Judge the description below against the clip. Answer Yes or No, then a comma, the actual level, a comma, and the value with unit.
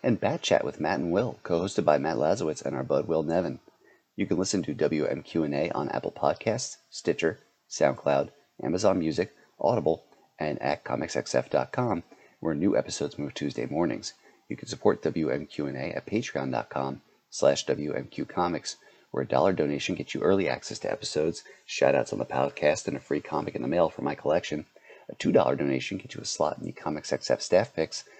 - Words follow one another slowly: No, average, 185 wpm